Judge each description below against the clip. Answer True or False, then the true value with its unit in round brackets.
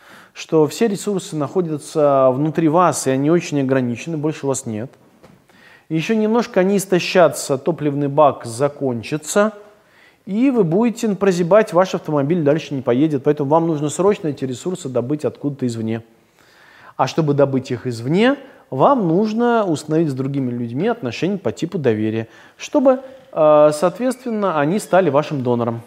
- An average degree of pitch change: False (6.5 semitones)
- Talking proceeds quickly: False (140 wpm)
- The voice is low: False (155 Hz)